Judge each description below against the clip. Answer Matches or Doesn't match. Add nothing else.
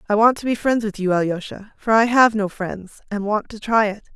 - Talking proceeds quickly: Matches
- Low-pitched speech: Doesn't match